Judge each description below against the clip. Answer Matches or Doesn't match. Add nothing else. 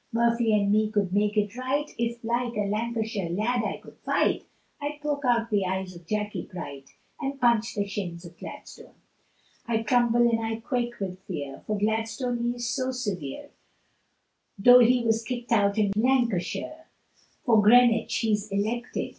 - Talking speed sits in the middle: Matches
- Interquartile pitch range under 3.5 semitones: Matches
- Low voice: Doesn't match